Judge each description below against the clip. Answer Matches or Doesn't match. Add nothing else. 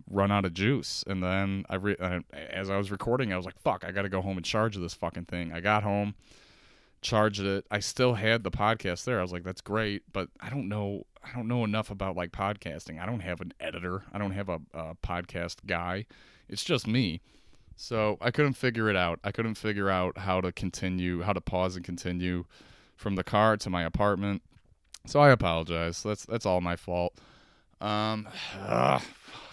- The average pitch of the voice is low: Matches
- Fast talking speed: Matches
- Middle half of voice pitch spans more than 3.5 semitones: Doesn't match